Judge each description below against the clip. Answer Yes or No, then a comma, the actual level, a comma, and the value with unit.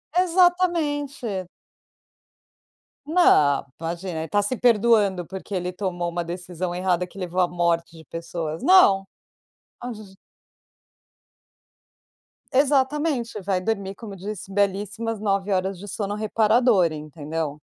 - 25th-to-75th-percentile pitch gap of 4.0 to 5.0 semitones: Yes, average, 4.7 semitones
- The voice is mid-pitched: No, high, 195 Hz